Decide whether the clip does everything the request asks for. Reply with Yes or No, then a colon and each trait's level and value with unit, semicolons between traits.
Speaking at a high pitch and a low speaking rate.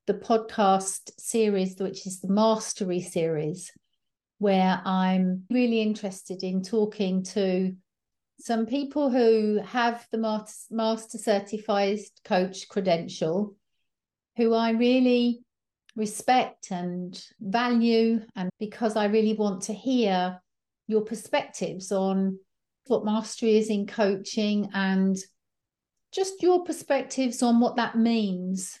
Yes: high, 215 Hz; slow, 110 wpm